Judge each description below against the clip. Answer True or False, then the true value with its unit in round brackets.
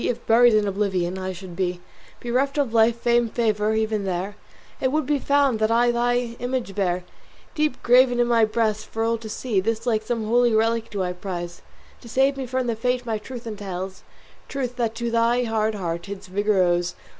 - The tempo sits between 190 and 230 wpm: True (200 wpm)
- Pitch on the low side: False (225 Hz)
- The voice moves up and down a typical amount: True (3.4 semitones)